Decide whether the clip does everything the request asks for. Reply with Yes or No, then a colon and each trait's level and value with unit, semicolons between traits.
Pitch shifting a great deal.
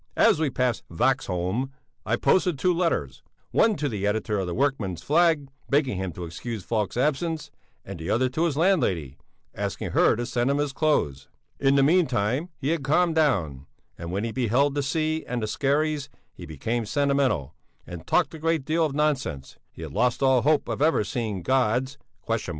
Yes: wide, 6.4 semitones